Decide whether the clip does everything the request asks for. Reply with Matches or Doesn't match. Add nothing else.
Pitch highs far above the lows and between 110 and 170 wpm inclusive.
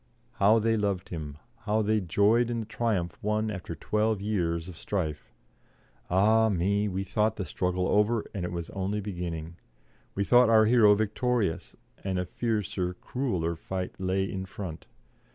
Doesn't match